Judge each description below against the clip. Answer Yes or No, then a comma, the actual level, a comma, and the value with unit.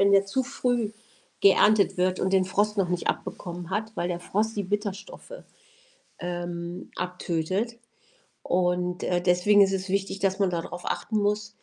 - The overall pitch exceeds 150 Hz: Yes, high, 190 Hz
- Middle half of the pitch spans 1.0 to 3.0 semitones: Yes, narrow, 2.6 semitones